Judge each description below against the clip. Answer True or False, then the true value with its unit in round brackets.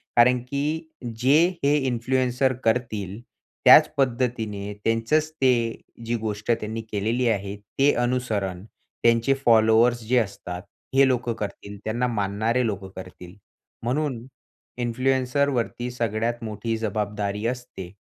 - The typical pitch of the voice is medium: False (115 Hz)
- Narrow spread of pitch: False (3.1 semitones)